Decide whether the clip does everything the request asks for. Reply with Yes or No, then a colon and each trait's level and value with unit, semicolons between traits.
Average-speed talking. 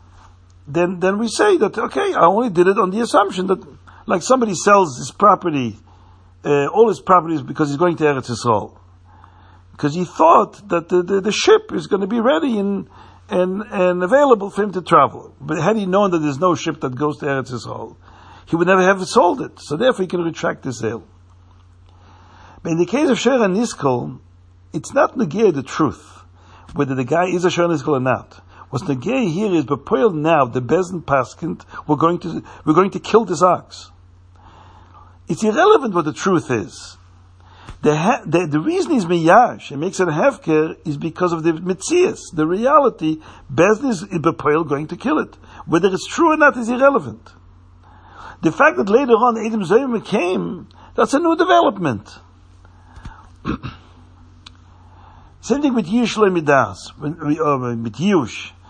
Yes: average, 175 wpm